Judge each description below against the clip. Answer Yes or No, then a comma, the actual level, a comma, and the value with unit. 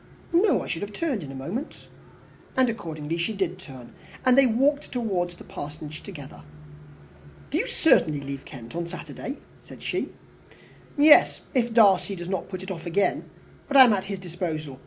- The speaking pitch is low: No, medium, 185 Hz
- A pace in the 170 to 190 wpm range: Yes, average, 180 wpm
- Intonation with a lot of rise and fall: Yes, wide, 6.9 semitones